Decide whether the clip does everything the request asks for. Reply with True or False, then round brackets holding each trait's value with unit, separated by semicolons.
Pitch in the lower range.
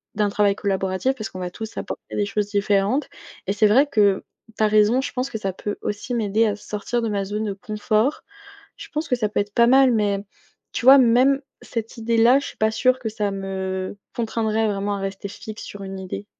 False (210 Hz)